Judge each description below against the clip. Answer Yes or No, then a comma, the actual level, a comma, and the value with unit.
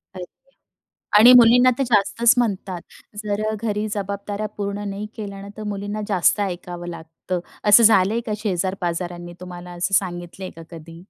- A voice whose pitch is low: No, high, 200 Hz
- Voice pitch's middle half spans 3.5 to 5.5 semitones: No, average, 3.1 semitones